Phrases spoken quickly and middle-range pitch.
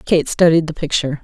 No: average, 195 wpm; medium, 155 Hz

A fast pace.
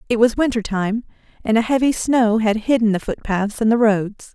Yes: fast, 220 wpm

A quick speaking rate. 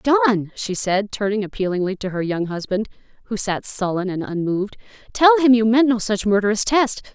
No: average, 185 wpm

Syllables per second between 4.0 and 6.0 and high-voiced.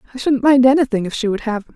No: 7.8 syllables/s; high, 245 Hz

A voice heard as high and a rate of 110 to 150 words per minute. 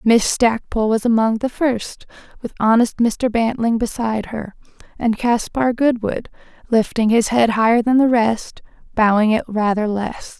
Yes: high, 230 Hz; average, 145 wpm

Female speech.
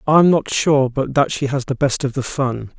No: male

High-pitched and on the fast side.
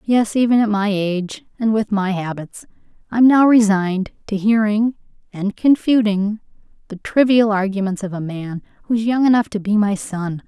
No: high, 210 Hz; average, 180 wpm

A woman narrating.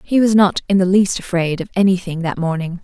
Yes: female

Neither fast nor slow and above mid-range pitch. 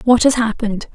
Yes: average, 190 wpm; high, 230 Hz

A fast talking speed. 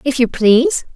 No: average, 190 wpm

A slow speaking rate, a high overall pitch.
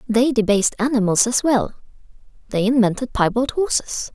Yes: slow, 130 wpm; high, 235 Hz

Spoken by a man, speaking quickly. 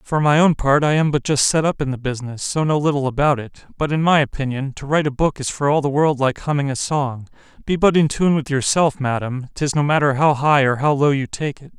Yes: male; fast, 260 wpm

